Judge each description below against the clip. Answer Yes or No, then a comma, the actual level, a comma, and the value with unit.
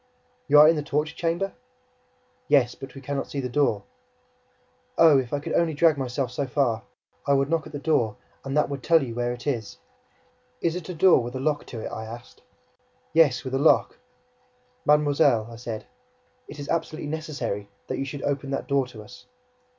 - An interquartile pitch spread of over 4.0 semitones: No, average, 3.7 semitones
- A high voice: No, medium, 140 Hz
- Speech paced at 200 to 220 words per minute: Yes, fast, 205 wpm